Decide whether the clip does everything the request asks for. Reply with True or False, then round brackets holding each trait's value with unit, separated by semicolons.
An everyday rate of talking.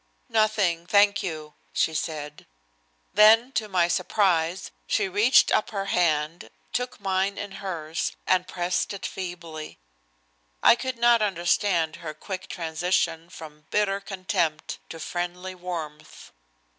False (125 wpm)